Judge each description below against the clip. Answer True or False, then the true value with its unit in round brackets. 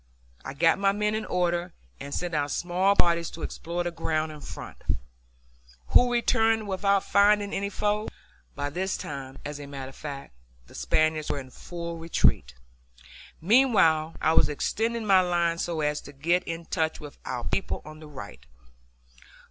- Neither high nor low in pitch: True (170 Hz)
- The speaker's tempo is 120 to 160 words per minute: False (170 wpm)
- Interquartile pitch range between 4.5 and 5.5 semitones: True (4.9 semitones)